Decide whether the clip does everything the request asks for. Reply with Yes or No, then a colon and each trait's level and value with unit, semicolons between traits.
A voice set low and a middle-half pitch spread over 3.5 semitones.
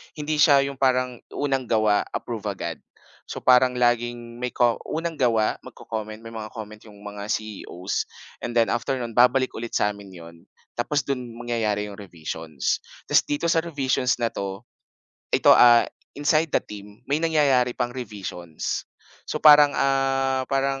Yes: low, 120 Hz; average, 4.2 semitones